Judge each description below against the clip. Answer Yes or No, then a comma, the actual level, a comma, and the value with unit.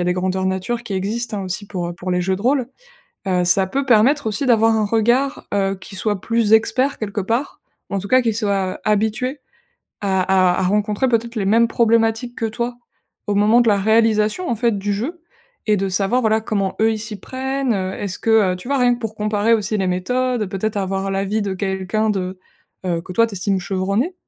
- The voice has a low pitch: No, high, 215 Hz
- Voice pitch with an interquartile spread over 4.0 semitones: No, average, 3.2 semitones